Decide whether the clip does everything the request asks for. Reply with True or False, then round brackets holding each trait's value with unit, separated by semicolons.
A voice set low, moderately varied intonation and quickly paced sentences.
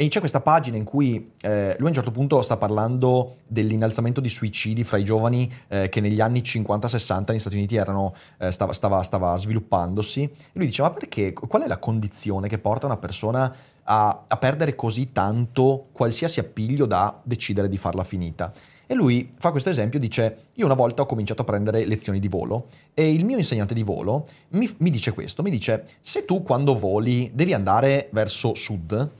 True (115 Hz; 4.4 semitones; 195 wpm)